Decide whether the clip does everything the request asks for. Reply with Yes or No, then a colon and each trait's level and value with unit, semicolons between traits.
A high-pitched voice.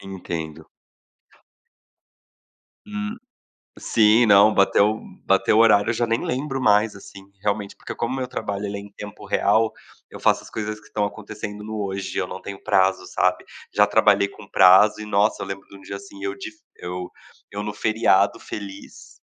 No: low, 105 Hz